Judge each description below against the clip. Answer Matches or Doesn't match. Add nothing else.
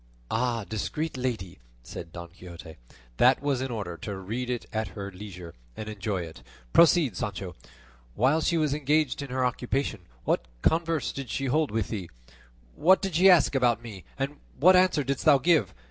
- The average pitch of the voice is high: Doesn't match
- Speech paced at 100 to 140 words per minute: Doesn't match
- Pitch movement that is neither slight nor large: Doesn't match